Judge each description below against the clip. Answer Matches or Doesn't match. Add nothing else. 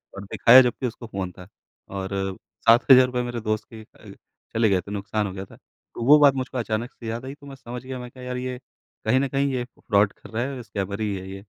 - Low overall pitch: Matches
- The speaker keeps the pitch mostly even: Doesn't match